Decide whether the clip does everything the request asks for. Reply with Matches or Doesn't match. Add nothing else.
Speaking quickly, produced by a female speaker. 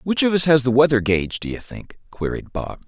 Doesn't match